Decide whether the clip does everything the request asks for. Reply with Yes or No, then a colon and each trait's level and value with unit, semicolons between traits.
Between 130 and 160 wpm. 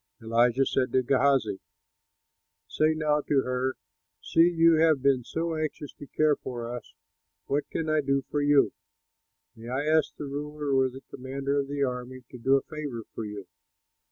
No: average, 175 wpm